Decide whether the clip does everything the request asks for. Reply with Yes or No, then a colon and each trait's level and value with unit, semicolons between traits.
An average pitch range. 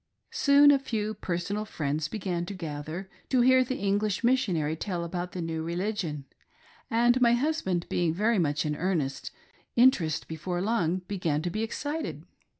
No: wide, 6.1 semitones